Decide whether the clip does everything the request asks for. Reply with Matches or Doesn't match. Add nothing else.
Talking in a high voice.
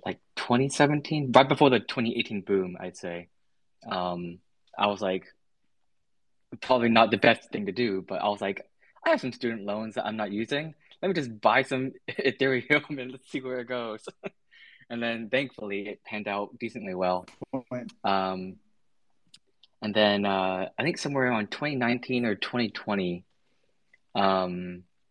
Doesn't match